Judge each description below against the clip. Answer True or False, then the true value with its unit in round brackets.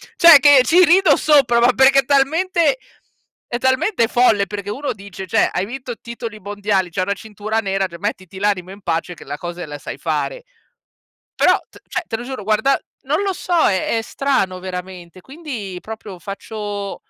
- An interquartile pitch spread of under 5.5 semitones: False (6.0 semitones)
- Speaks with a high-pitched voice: True (215 Hz)